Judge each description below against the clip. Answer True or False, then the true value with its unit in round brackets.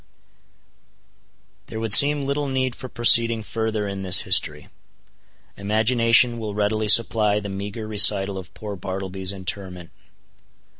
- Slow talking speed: True (120 wpm)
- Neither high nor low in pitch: False (105 Hz)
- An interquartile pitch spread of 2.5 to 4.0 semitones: True (3.0 semitones)